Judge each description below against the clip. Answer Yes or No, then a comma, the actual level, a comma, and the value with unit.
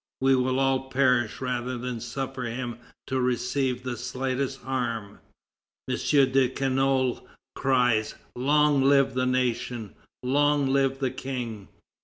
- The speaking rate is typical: No, slow, 125 wpm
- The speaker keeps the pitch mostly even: Yes, narrow, 1.5 semitones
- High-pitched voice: No, low, 130 Hz